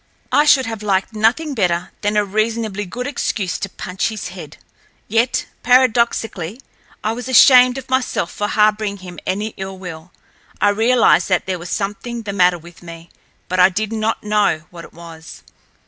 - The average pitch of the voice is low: No, high, 210 Hz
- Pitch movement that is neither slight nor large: Yes, average, 3.9 semitones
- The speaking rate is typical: Yes, average, 175 wpm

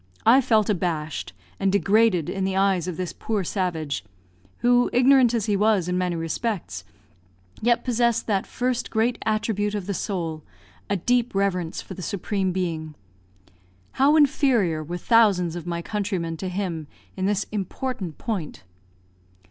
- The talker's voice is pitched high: Yes, high, 195 Hz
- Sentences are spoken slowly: No, average, 150 wpm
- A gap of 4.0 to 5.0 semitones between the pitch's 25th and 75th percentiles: Yes, average, 4.5 semitones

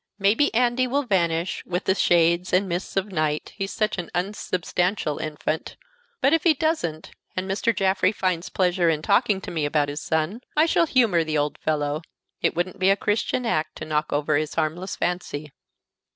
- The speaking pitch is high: No, medium, 180 Hz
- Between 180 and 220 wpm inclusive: Yes, average, 185 wpm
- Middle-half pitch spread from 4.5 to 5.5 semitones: Yes, average, 4.8 semitones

